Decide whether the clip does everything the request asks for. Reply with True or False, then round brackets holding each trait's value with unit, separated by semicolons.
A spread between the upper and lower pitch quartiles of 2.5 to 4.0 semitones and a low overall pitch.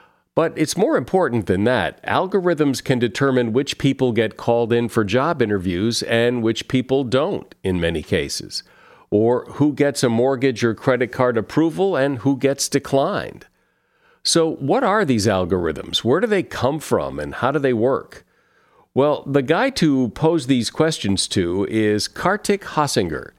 False (4.4 semitones; 130 Hz)